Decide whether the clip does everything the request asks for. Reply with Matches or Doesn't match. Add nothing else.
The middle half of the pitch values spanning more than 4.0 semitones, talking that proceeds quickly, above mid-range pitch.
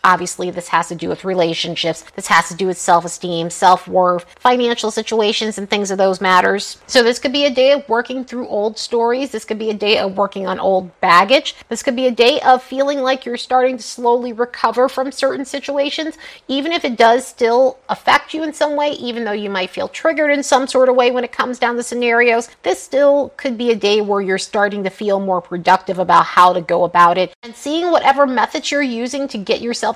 Matches